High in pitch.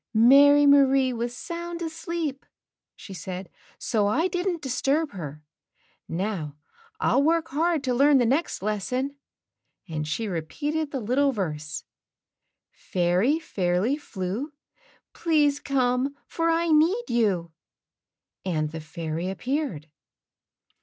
Yes: very high, 255 Hz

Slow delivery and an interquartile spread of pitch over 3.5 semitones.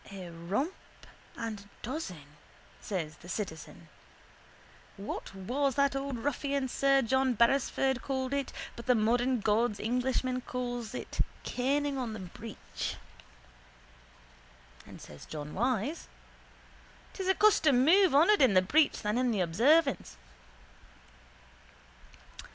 Yes: slow, 115 wpm; average, 4.9 semitones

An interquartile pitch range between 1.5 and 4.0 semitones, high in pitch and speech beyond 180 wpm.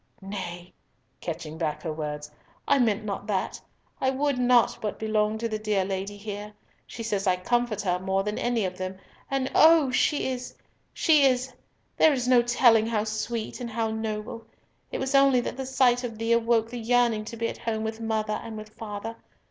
Yes: average, 3.0 semitones; high, 220 Hz; average, 195 wpm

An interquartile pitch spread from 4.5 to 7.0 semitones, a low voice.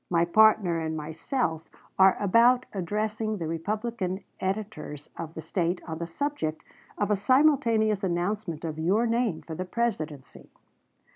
No: average, 4.8 semitones; high, 190 Hz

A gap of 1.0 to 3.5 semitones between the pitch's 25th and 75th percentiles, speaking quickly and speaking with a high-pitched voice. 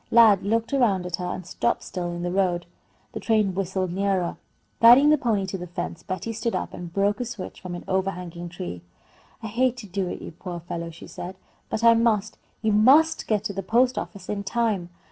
No: average, 4.2 semitones; fast, 220 wpm; high, 195 Hz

